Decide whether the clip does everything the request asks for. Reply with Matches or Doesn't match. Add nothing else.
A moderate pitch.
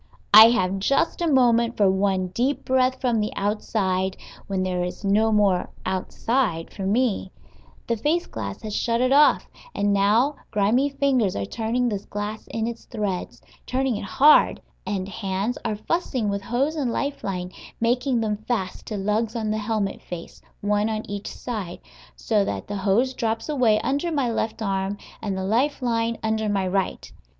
Doesn't match